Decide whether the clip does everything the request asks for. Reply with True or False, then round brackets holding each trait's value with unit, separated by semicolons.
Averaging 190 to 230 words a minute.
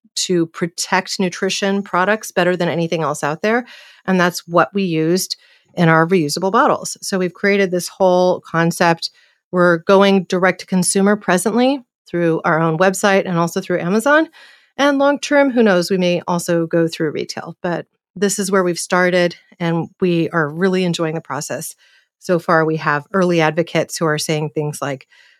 False (175 wpm)